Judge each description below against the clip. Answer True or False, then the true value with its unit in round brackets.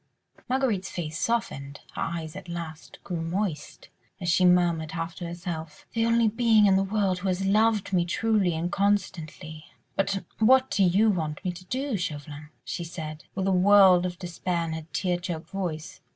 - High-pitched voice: False (180 Hz)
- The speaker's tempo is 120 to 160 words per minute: False (180 wpm)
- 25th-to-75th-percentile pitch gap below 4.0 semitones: True (3.5 semitones)